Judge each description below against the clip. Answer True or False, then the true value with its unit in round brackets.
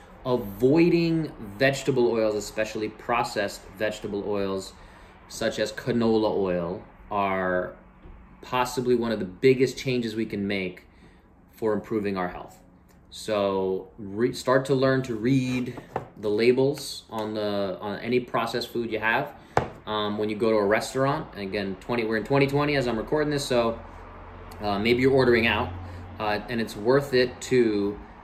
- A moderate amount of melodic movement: True (4.0 semitones)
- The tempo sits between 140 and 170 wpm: True (150 wpm)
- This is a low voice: True (110 Hz)